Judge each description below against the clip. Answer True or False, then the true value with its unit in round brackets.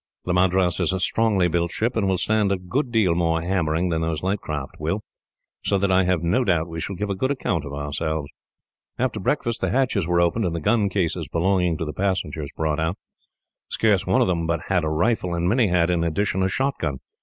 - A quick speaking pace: True (230 wpm)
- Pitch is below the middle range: True (90 Hz)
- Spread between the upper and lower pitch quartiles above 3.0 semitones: True (3.4 semitones)